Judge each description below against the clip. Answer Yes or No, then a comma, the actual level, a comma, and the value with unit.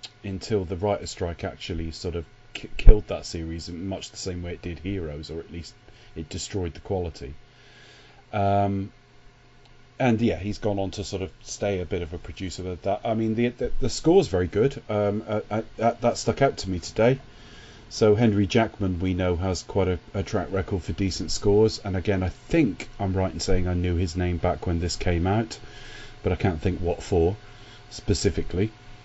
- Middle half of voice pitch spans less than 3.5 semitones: Yes, average, 3.1 semitones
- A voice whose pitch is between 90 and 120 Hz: Yes, very low, 95 Hz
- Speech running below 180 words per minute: No, fast, 205 wpm